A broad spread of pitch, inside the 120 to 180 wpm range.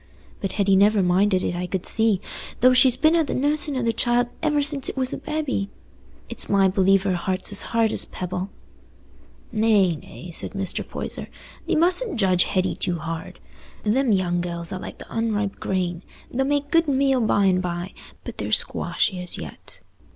No: wide, 5.9 semitones; average, 190 wpm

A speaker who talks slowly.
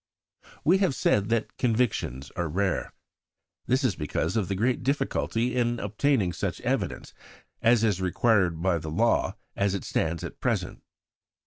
No: average, 155 wpm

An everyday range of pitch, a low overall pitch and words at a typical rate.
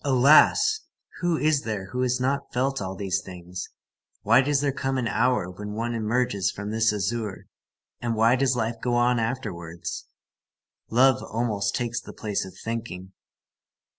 Yes: average, 4.0 semitones; low, 115 Hz; average, 160 wpm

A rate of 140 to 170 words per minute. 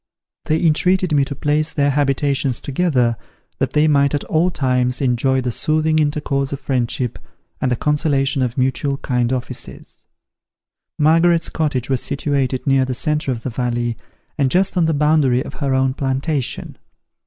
Yes: average, 160 wpm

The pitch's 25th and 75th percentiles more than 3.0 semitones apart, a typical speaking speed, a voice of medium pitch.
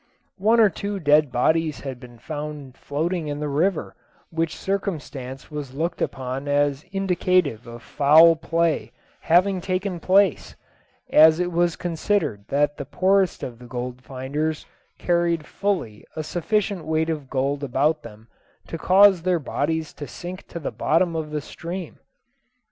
Yes: average, 4.0 semitones; average, 150 wpm; medium, 160 Hz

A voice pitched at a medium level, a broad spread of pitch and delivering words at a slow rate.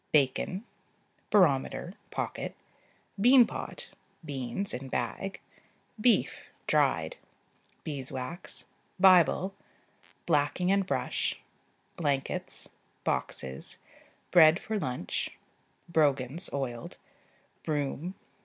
Yes: medium, 155 Hz; wide, 5.8 semitones; slow, 75 wpm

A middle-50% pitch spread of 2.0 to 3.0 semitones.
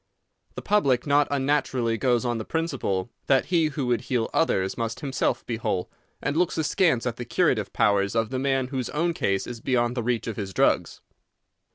No: average, 3.9 semitones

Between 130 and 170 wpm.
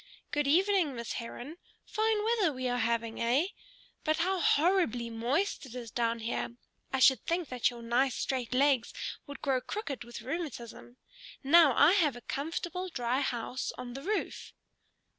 Yes: average, 160 wpm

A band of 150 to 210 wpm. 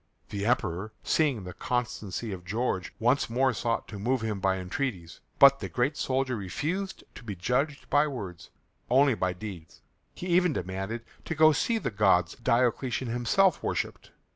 Yes: average, 165 wpm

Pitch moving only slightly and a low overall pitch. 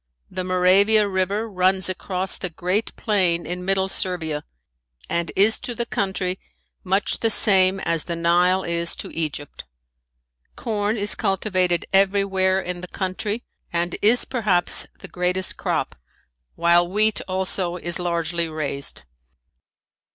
No: narrow, 2.3 semitones; medium, 185 Hz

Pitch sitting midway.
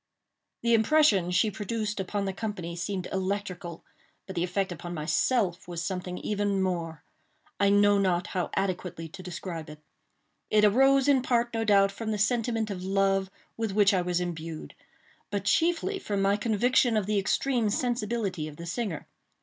No: high, 200 Hz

